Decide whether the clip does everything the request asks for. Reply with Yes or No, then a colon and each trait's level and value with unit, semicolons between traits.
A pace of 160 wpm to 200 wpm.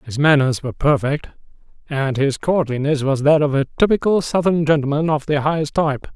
Yes: average, 175 wpm